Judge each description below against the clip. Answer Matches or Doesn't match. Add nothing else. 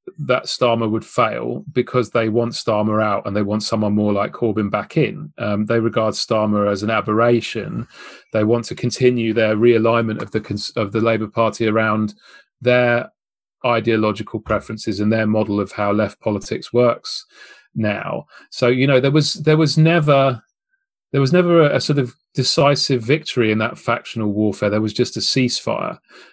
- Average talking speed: Matches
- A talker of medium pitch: Doesn't match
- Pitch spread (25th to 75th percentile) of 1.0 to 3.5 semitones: Matches